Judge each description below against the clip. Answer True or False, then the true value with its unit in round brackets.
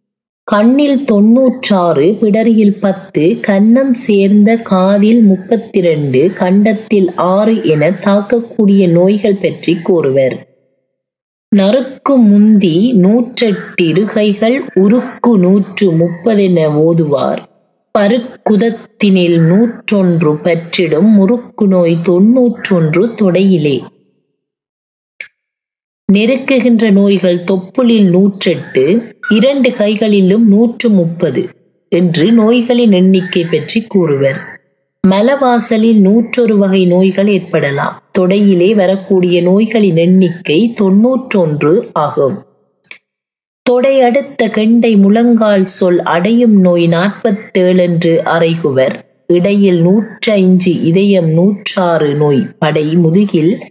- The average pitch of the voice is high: True (195 Hz)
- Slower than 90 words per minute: True (80 wpm)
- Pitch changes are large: False (4.2 semitones)